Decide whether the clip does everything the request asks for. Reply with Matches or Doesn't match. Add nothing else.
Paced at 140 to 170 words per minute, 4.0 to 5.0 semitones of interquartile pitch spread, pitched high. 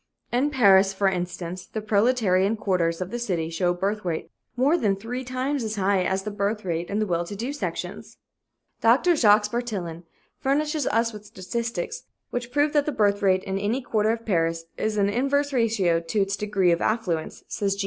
Doesn't match